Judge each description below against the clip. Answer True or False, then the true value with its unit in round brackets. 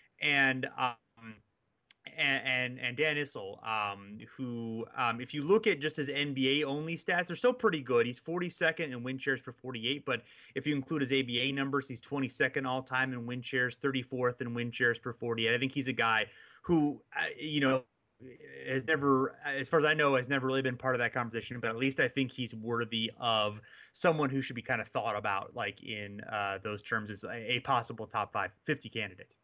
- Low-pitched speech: True (130 Hz)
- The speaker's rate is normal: False (210 wpm)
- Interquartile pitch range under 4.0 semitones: True (2.9 semitones)